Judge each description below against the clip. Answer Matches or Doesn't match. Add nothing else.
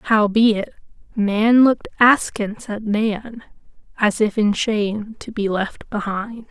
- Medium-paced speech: Doesn't match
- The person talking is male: Doesn't match